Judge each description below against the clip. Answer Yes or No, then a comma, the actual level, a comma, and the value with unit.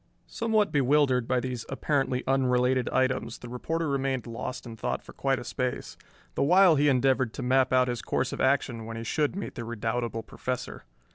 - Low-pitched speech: Yes, low, 130 Hz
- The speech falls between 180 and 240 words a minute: Yes, average, 190 wpm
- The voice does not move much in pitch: Yes, narrow, 2.3 semitones